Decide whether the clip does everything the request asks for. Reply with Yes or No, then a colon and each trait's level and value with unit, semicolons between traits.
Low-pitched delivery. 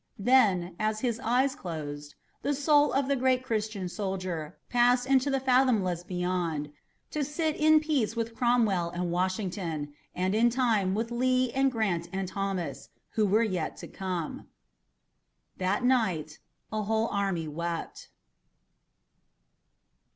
No: high, 215 Hz